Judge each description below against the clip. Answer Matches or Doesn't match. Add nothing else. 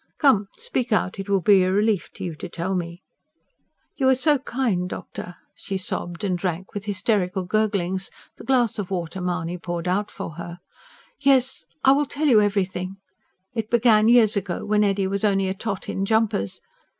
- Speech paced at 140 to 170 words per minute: Doesn't match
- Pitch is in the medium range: Doesn't match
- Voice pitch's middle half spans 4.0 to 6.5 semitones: Doesn't match